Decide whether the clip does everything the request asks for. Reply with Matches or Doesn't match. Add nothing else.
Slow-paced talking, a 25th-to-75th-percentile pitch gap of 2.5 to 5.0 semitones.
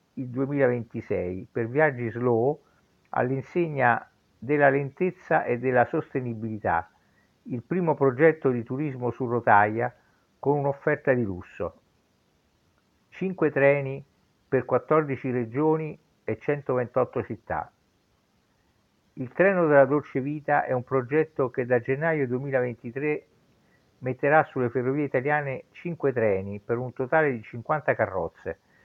Matches